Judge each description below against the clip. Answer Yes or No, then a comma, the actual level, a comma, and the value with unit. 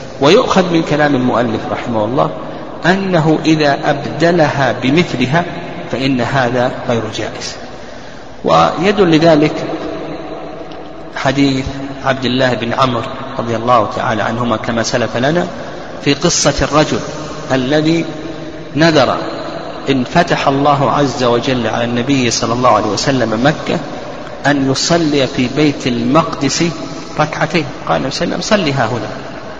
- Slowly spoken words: No, average, 110 wpm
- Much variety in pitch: No, average, 3.6 semitones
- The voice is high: No, medium, 140 Hz